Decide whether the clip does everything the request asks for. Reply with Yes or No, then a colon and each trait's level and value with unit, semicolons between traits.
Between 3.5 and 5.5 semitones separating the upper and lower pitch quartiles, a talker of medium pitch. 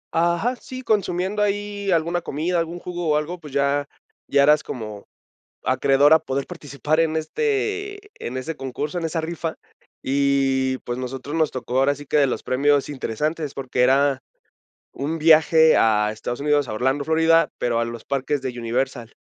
Yes: average, 3.9 semitones; medium, 145 Hz